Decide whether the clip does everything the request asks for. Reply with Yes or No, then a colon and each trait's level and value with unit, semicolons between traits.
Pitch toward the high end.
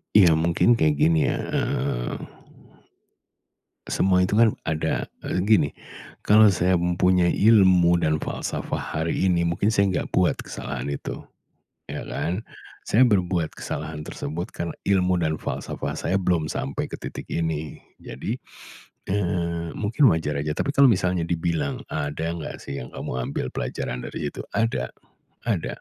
No: very low, 85 Hz